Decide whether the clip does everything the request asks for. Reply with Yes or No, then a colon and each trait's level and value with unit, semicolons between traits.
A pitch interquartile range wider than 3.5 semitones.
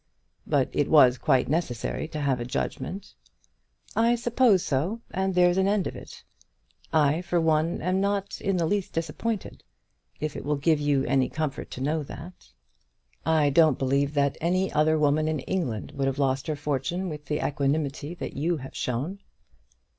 Yes: average, 4.3 semitones